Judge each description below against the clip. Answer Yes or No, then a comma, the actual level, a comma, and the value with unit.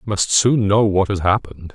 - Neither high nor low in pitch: No, low, 100 Hz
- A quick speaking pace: Yes, fast, 240 wpm